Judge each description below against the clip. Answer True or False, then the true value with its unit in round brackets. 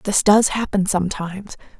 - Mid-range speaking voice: False (195 Hz)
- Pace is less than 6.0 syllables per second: True (5.1 syllables/s)